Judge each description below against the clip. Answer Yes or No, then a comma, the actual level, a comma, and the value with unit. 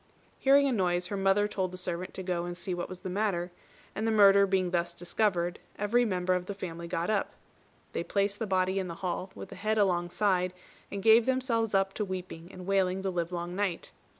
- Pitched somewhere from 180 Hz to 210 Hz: Yes, high, 190 Hz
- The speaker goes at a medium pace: No, fast, 215 wpm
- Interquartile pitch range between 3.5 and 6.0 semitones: No, narrow, 2.4 semitones